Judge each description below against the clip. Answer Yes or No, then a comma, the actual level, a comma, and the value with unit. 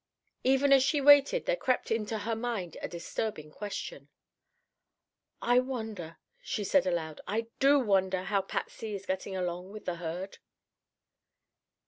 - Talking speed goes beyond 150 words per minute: No, average, 140 wpm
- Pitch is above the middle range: Yes, high, 210 Hz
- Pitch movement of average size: No, wide, 5.7 semitones